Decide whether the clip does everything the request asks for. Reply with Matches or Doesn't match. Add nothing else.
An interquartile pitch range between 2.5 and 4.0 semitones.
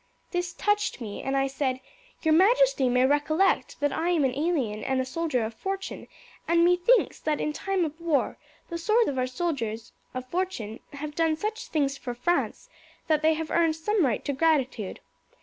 Doesn't match